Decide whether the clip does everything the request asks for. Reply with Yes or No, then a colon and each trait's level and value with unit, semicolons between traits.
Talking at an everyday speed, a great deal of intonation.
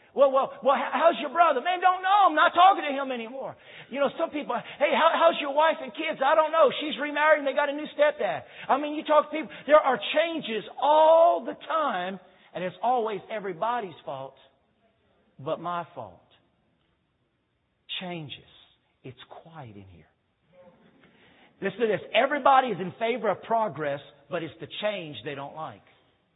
Yes: average, 180 wpm; wide, 8.8 semitones